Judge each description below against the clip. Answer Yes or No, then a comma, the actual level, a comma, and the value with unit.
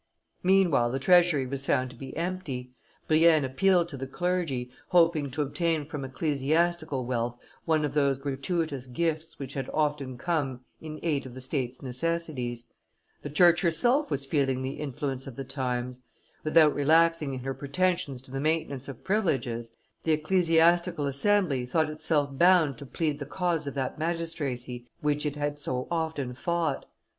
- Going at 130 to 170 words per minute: Yes, average, 160 wpm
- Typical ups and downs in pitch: Yes, average, 3.9 semitones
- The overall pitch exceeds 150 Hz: No, medium, 145 Hz